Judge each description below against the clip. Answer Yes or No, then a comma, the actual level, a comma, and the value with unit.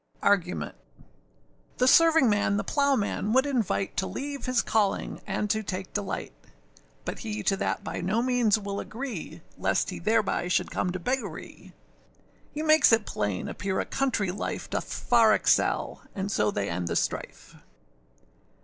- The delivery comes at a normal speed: Yes, average, 160 wpm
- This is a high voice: Yes, high, 215 Hz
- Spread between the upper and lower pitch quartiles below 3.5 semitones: No, average, 4.8 semitones